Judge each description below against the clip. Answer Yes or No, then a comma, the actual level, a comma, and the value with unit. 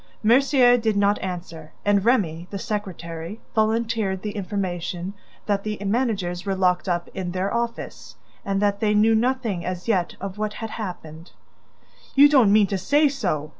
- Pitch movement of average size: Yes, average, 3.6 semitones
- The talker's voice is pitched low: No, high, 200 Hz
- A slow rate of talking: No, average, 165 wpm